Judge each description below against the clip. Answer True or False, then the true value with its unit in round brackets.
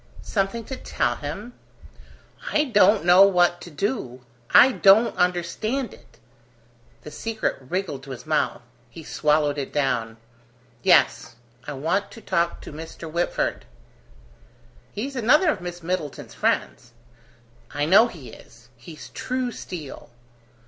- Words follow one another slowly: True (130 wpm)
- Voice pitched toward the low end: False (175 Hz)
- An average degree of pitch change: False (6.7 semitones)